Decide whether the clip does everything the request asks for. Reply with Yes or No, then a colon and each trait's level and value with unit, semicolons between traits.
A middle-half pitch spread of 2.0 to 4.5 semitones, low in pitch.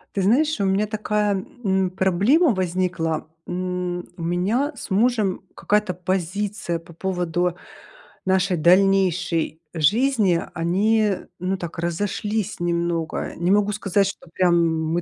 No: average, 3.1 semitones; medium, 185 Hz